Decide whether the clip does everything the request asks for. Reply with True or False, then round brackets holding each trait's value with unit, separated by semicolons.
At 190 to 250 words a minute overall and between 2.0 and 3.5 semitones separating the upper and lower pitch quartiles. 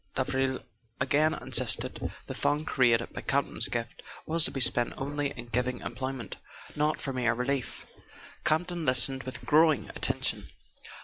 False (140 wpm; 2.8 semitones)